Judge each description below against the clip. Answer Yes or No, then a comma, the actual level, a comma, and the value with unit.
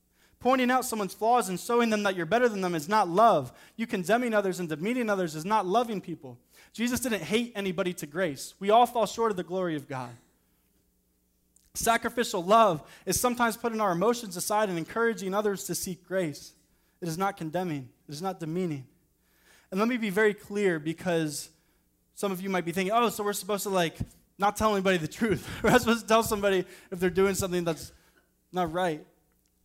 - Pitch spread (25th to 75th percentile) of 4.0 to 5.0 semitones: Yes, average, 4.7 semitones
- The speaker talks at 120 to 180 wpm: No, average, 200 wpm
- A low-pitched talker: No, high, 195 Hz